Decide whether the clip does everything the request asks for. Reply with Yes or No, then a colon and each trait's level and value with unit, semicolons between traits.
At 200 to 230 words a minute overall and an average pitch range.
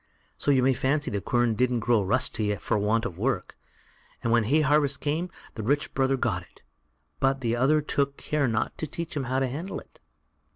Yes: fast, 205 wpm; average, 3.8 semitones